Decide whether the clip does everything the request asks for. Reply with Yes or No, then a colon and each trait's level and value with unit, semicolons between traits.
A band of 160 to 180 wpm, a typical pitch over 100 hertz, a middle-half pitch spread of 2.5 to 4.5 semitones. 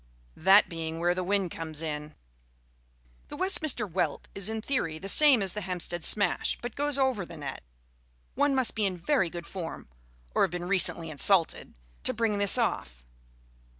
No: average, 175 wpm; high, 190 Hz; average, 5.0 semitones